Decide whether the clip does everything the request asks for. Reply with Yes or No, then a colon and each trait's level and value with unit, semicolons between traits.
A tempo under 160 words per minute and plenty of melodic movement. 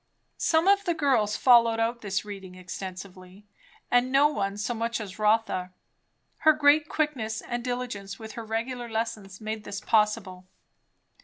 No: average, 150 wpm; average, 3.7 semitones